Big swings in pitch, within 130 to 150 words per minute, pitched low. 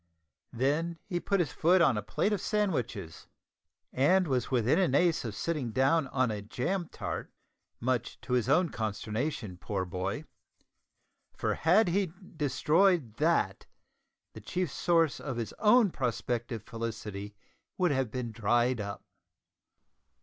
Yes: wide, 7.0 semitones; average, 140 wpm; low, 130 Hz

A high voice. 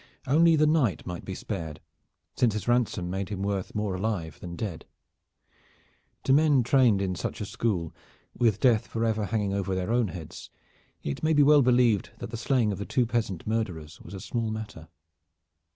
No: low, 105 Hz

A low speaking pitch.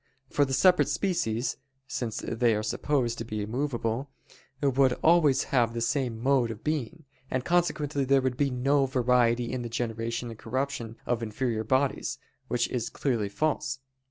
Yes: low, 125 Hz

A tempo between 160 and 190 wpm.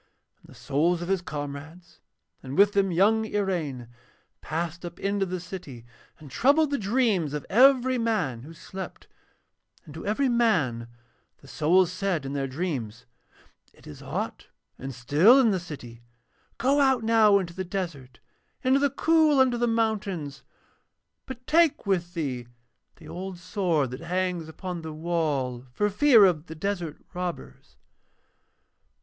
No: average, 150 wpm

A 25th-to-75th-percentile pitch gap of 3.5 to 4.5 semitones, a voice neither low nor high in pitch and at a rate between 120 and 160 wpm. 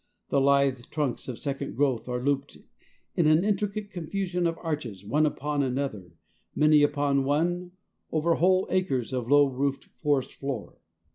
Yes: average, 3.8 semitones; medium, 145 Hz; average, 150 wpm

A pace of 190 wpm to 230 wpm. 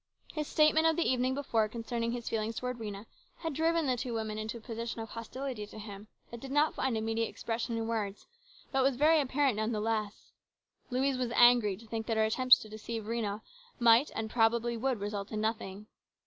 Yes: fast, 205 wpm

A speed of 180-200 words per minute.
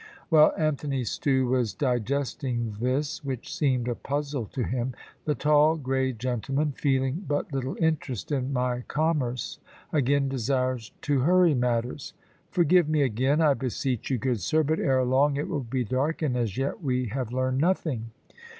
No: average, 160 wpm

